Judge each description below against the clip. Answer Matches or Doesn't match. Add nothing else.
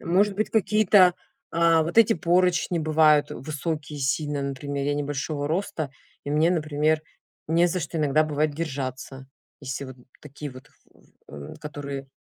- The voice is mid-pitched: Matches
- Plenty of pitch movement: Doesn't match